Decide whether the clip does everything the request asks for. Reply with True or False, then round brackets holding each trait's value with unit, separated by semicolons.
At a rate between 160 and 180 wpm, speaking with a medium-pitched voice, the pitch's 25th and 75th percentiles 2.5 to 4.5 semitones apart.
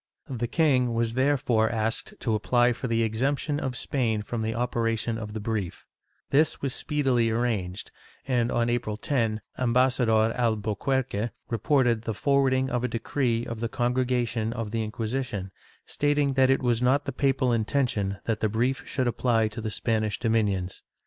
False (165 wpm; 120 Hz; 2.8 semitones)